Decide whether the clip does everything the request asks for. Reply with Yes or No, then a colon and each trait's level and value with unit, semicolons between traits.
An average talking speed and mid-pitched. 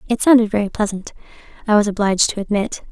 No: average, 185 wpm; high, 210 Hz